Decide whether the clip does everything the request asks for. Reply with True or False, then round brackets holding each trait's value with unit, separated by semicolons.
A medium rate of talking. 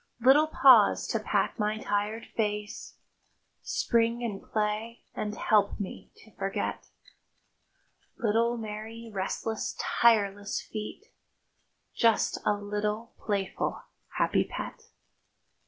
False (100 wpm)